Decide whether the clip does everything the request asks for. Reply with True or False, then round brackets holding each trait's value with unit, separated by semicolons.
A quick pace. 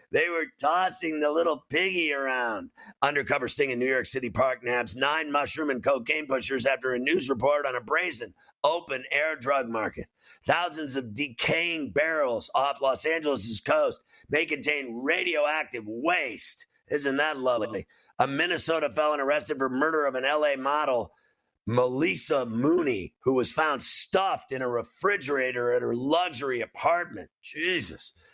False (150 wpm)